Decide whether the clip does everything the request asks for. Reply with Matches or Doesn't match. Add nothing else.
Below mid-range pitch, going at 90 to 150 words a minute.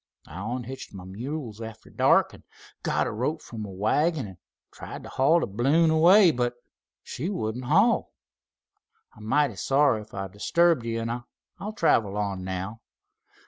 Doesn't match